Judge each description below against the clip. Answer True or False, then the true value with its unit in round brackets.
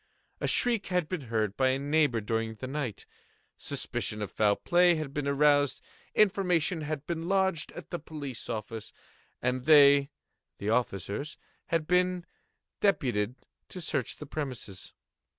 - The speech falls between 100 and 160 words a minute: True (145 wpm)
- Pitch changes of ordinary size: False (5.9 semitones)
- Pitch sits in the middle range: True (145 Hz)